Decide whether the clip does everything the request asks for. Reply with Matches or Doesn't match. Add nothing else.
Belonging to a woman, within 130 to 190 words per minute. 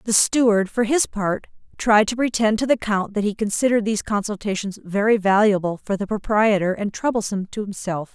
Matches